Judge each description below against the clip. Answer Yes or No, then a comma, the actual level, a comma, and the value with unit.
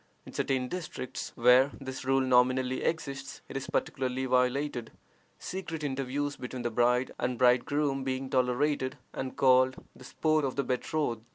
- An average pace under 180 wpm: Yes, average, 150 wpm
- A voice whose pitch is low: Yes, low, 130 Hz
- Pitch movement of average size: No, narrow, 1.7 semitones